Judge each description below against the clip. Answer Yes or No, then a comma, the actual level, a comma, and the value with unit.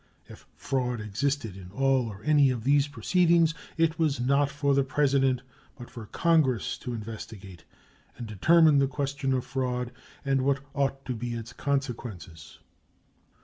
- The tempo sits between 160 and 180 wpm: No, average, 150 wpm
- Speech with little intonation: No, average, 3.4 semitones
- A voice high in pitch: No, low, 135 Hz